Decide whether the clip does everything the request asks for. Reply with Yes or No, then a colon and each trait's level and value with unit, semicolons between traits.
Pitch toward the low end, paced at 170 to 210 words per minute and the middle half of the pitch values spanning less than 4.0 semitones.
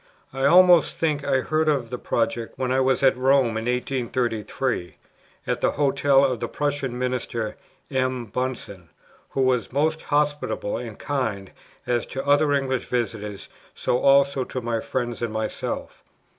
No: low, 130 Hz; average, 155 wpm; average, 2.9 semitones